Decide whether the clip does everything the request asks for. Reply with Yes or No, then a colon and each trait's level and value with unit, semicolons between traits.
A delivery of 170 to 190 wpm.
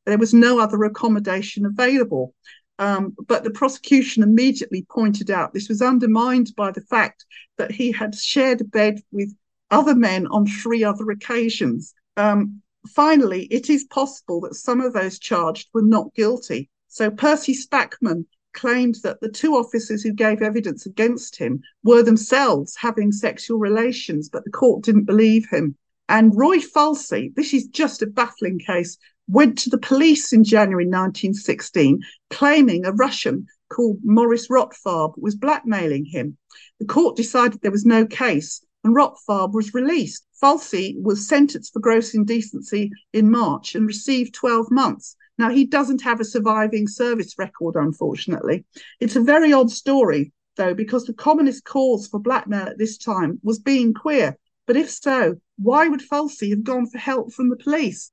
No: average, 160 wpm